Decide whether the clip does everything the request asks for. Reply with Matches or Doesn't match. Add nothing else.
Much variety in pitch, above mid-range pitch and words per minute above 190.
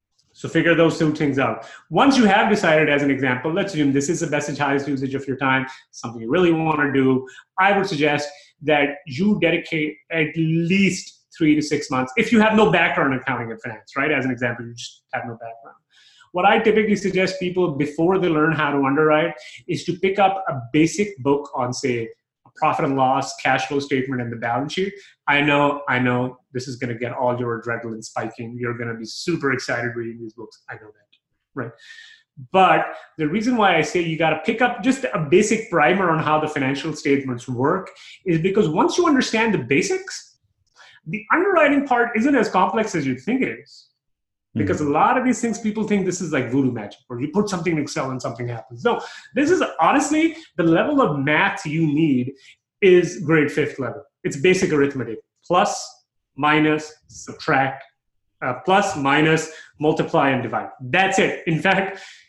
Doesn't match